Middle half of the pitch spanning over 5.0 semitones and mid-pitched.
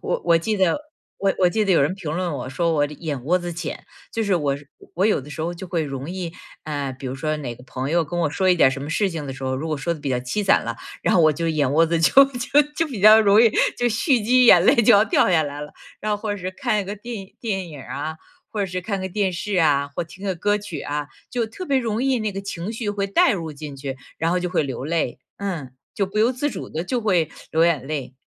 Yes: wide, 5.5 semitones; medium, 175 Hz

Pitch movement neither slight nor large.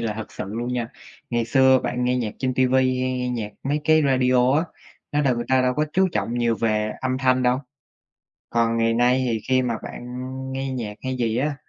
No: narrow, 1.9 semitones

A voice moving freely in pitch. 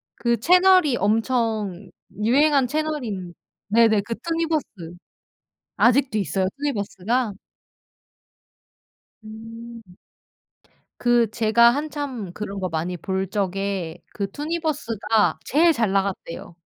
Yes: wide, 5.9 semitones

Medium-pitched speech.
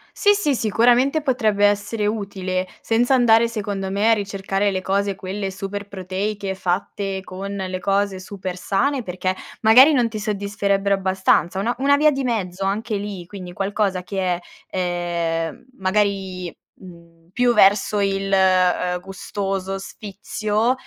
No: high, 200 Hz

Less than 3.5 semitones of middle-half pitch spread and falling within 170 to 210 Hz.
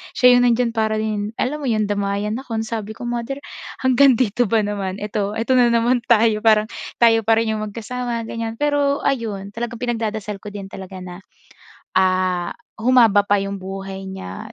No: average, 3.0 semitones; high, 220 Hz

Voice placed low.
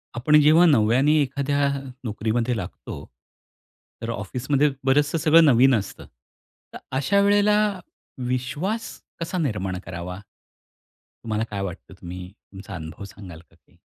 Yes: low, 125 Hz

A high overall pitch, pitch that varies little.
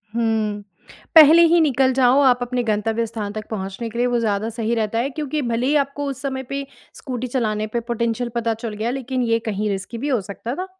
No: high, 235 Hz; average, 3.2 semitones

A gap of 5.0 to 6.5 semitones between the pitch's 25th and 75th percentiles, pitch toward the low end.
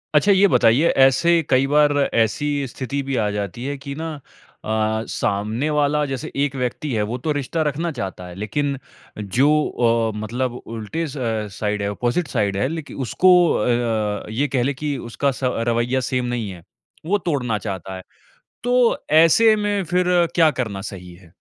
Yes: wide, 5.5 semitones; low, 130 Hz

